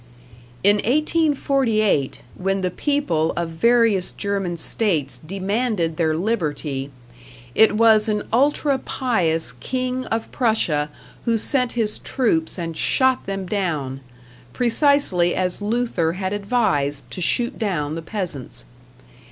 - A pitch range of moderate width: No, wide, 6.4 semitones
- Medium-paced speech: No, slow, 120 wpm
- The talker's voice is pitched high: Yes, high, 200 Hz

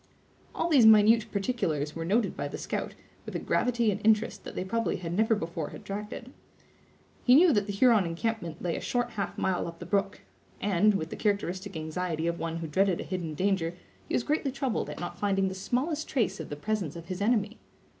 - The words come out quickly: Yes, fast, 210 wpm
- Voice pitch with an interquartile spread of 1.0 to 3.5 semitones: No, average, 4.7 semitones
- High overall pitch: Yes, high, 200 Hz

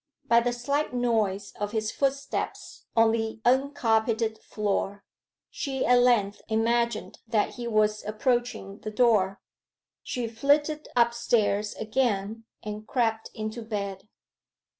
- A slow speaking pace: Yes, slow, 120 wpm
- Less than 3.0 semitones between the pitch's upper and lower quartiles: Yes, narrow, 2.4 semitones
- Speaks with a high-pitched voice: Yes, high, 225 Hz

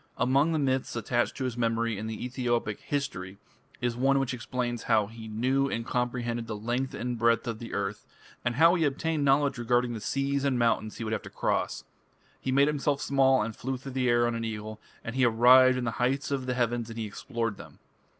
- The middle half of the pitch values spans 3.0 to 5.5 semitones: No, narrow, 2.6 semitones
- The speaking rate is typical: No, fast, 220 wpm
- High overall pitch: No, low, 120 Hz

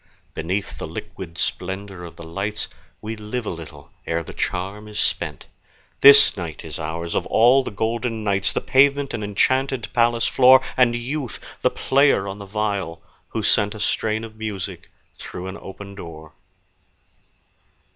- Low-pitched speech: Yes, low, 105 Hz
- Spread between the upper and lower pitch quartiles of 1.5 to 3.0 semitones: No, average, 3.9 semitones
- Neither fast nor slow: Yes, average, 160 wpm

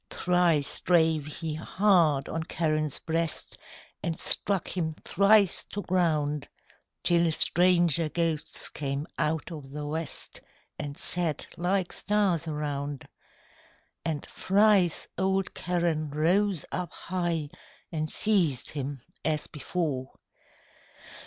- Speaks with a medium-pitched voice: Yes, medium, 165 Hz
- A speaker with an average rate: No, slow, 105 wpm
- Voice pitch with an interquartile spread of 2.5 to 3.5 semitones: Yes, average, 3.0 semitones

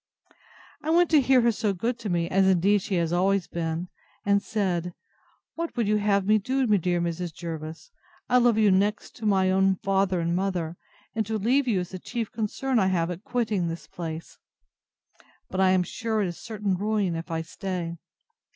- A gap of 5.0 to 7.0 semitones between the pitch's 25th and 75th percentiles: No, average, 3.9 semitones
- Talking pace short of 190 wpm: No, average, 200 wpm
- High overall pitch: Yes, high, 195 Hz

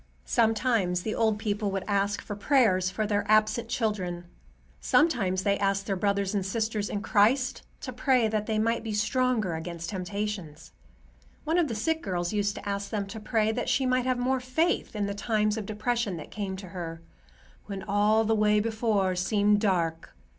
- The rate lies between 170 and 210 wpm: Yes, average, 185 wpm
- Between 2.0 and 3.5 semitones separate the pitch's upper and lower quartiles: Yes, narrow, 2.4 semitones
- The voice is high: Yes, high, 210 Hz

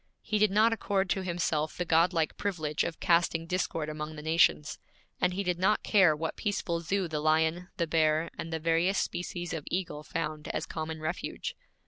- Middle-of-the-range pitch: Yes, medium, 165 Hz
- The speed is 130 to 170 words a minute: No, average, 185 wpm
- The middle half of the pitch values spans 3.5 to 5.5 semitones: No, average, 2.8 semitones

